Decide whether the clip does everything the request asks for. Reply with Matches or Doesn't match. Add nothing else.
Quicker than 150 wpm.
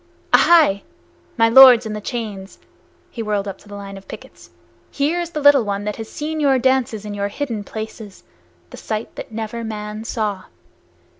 Matches